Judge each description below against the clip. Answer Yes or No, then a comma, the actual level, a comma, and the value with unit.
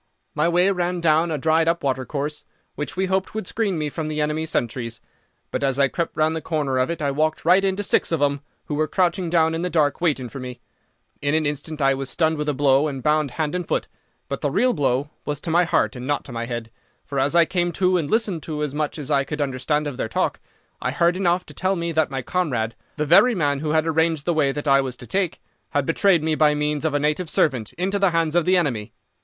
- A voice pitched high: No, medium, 155 Hz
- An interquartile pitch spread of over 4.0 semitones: No, average, 3.3 semitones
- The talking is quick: Yes, fast, 255 wpm